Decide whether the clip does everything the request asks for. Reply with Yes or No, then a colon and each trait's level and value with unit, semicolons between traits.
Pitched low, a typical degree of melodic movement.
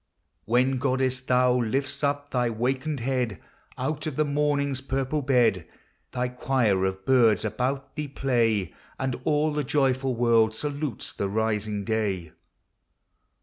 Yes: low, 130 Hz; average, 3.7 semitones